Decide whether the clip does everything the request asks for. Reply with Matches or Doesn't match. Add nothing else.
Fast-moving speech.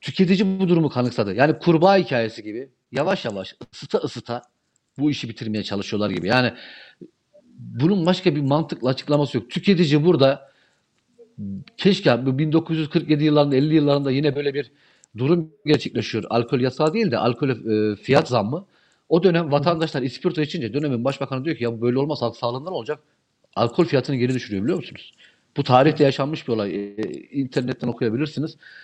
Doesn't match